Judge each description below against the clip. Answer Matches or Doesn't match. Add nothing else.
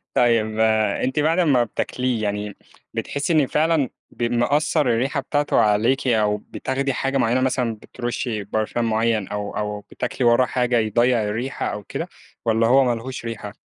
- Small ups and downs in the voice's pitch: Doesn't match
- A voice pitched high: Doesn't match